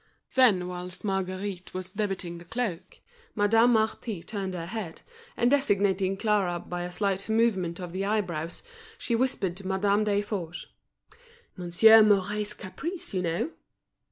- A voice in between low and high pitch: No, high, 195 Hz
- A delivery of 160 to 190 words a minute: No, slow, 135 wpm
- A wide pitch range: No, average, 3.1 semitones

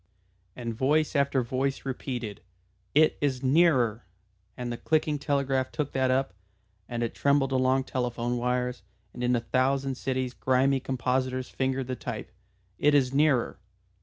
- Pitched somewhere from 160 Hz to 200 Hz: No, low, 130 Hz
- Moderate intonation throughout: No, narrow, 1.8 semitones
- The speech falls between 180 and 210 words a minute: No, average, 150 wpm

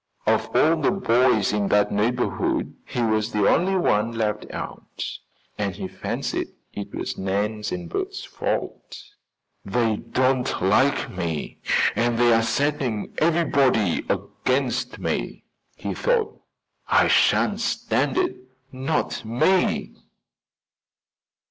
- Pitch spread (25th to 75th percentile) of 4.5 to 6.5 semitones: Yes, average, 4.8 semitones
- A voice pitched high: No, low, 115 Hz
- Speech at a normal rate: No, slow, 115 wpm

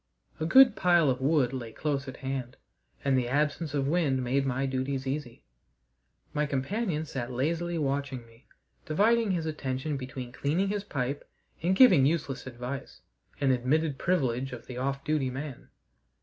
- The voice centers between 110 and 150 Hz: Yes, medium, 140 Hz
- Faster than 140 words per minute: Yes, average, 160 wpm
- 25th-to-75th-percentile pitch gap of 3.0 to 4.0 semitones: Yes, average, 3.3 semitones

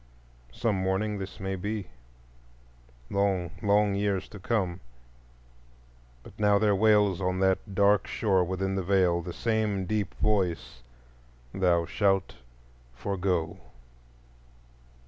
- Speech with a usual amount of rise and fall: No, narrow, 2.0 semitones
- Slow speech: Yes, slow, 110 wpm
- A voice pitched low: Yes, very low, 95 Hz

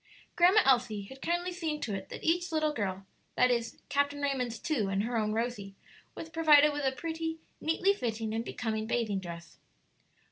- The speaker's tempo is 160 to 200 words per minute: Yes, average, 180 wpm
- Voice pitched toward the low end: No, very high, 250 Hz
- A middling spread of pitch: No, wide, 6.6 semitones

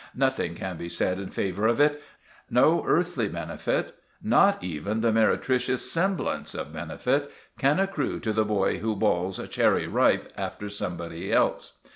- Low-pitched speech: Yes, low, 110 Hz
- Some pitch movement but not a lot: No, wide, 5.8 semitones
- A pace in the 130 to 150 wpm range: Yes, average, 140 wpm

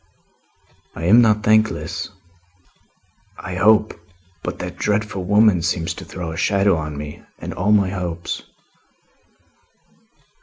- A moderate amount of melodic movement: Yes, average, 3.6 semitones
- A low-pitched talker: Yes, very low, 95 Hz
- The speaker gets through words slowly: Yes, slow, 125 wpm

